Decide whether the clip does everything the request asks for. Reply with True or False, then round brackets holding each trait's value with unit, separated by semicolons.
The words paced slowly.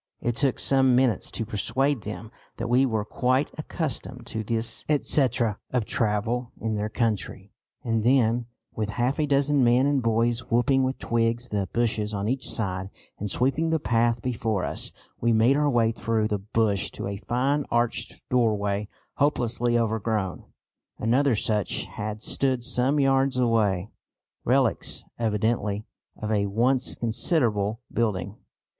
False (150 wpm)